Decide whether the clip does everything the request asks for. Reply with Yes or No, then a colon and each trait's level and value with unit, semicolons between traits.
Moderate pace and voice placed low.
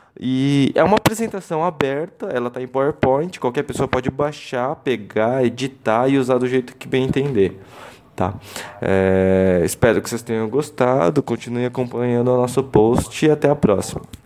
Yes: average, 160 wpm; low, 130 Hz